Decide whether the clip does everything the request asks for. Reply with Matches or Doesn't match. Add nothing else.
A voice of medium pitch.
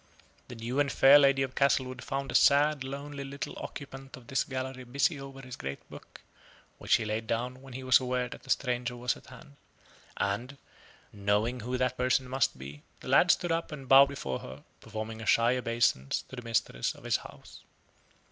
Doesn't match